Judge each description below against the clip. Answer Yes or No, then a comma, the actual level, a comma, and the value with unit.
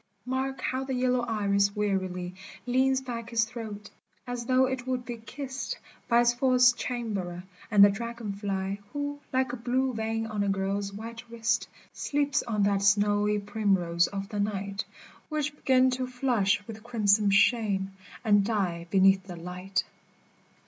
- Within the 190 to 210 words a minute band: No, average, 155 wpm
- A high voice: Yes, high, 220 Hz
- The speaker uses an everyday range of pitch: Yes, average, 3.8 semitones